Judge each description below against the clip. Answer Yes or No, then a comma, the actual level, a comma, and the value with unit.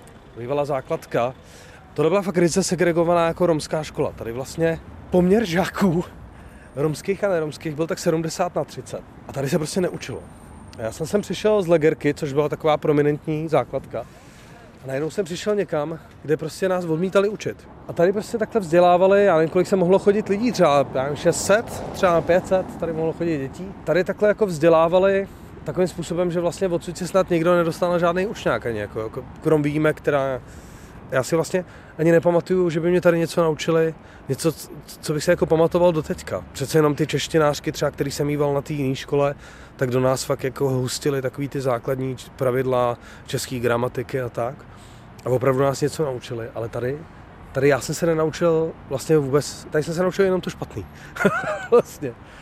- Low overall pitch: No, medium, 160 Hz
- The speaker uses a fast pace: Yes, fast, 180 wpm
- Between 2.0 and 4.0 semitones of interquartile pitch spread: No, average, 4.7 semitones